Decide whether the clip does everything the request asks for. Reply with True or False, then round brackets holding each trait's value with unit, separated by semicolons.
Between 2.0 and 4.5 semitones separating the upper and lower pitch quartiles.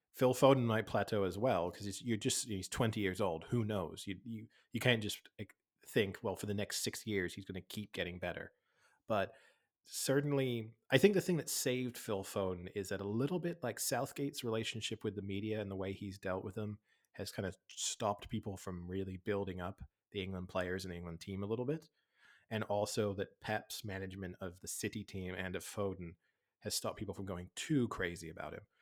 True (3.5 semitones)